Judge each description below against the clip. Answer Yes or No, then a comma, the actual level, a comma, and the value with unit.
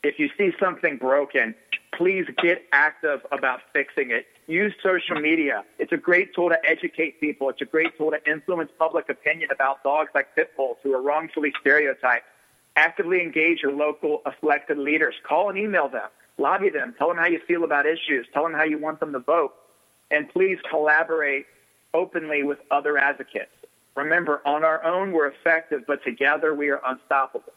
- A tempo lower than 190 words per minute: Yes, average, 180 wpm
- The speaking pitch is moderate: Yes, medium, 155 Hz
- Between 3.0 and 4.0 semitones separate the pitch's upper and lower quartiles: Yes, average, 3.5 semitones